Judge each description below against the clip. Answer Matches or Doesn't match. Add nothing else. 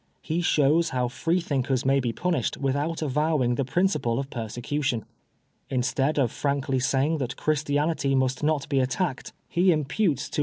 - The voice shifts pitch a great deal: Doesn't match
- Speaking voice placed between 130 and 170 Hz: Matches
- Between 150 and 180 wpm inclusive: Matches